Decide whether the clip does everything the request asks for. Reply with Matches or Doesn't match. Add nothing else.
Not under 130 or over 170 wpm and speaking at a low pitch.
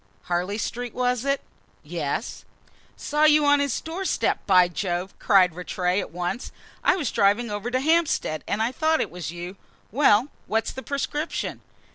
Doesn't match